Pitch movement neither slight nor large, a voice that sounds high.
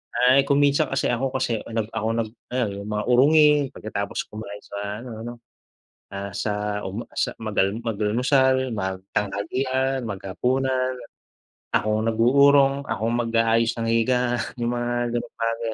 No: average, 3.6 semitones; low, 115 Hz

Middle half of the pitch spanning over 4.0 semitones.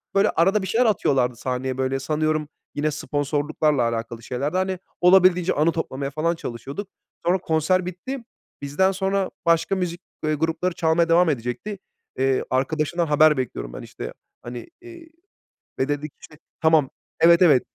Yes: average, 4.9 semitones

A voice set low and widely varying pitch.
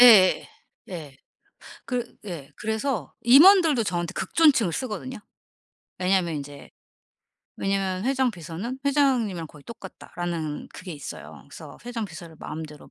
No: high, 195 Hz; wide, 6.7 semitones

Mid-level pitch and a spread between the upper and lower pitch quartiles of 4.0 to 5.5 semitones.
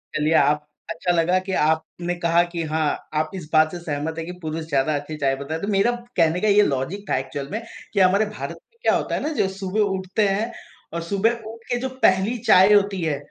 Yes: medium, 175 Hz; average, 4.3 semitones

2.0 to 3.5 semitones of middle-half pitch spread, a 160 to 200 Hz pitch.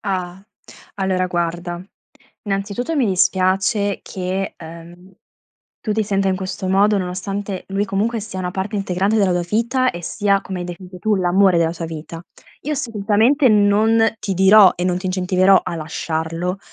Yes: narrow, 2.4 semitones; high, 190 Hz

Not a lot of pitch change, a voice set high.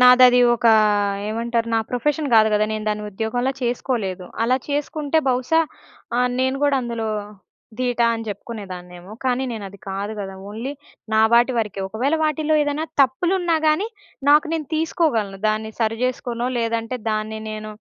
No: average, 3.9 semitones; high, 235 Hz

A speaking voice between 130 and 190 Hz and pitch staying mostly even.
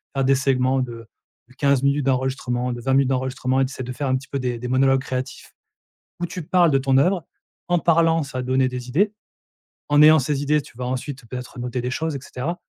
Yes: low, 135 Hz; narrow, 2.2 semitones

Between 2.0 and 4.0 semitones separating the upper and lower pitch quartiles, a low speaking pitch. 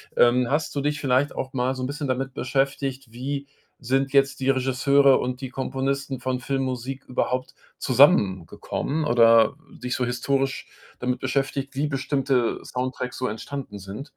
No: narrow, 1.6 semitones; low, 130 Hz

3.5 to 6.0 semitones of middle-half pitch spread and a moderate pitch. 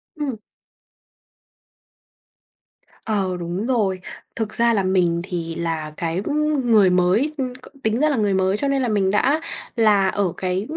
No: average, 5.0 semitones; high, 205 Hz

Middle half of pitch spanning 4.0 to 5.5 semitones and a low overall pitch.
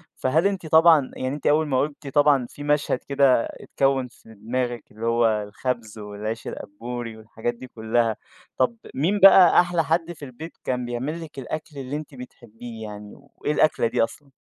Yes: average, 4.6 semitones; low, 130 Hz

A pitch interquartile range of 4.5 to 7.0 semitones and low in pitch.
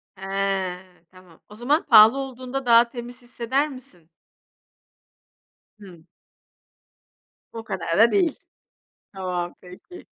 No: wide, 5.4 semitones; high, 225 Hz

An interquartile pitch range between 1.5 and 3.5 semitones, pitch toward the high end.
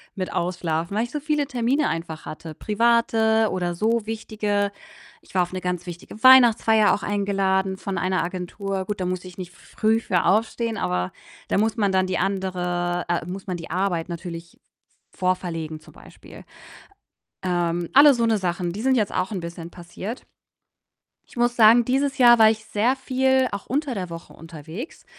No: average, 4.4 semitones; high, 195 Hz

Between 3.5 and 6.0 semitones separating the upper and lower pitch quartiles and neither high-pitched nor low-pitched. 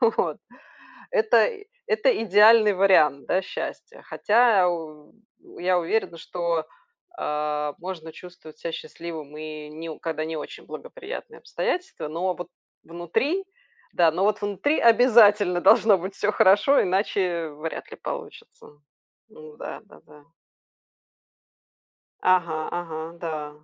Yes: average, 5.0 semitones; medium, 175 Hz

